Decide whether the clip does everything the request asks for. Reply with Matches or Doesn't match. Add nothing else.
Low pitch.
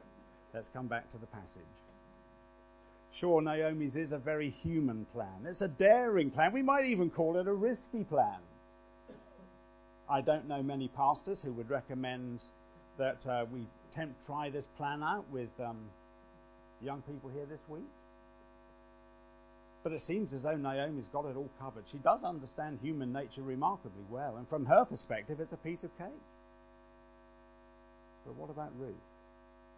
Doesn't match